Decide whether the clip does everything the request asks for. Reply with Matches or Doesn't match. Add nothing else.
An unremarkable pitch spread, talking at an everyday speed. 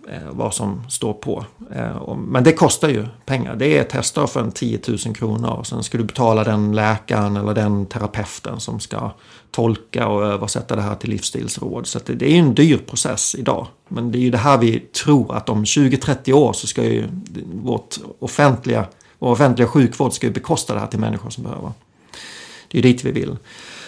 Doesn't match